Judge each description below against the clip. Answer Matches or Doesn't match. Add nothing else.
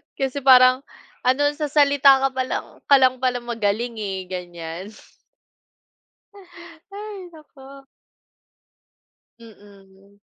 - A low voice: Doesn't match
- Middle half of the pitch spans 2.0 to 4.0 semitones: Doesn't match